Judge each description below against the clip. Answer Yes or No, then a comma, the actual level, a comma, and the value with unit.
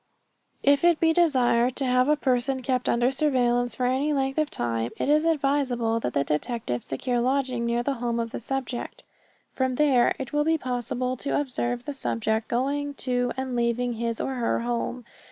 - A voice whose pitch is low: No, very high, 250 Hz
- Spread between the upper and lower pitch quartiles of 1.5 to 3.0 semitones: Yes, narrow, 2.5 semitones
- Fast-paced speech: No, average, 190 wpm